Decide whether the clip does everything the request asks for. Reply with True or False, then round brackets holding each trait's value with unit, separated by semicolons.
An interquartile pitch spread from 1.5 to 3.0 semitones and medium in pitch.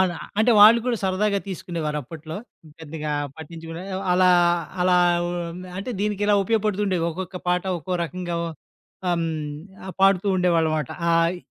True (2.7 semitones; 180 Hz)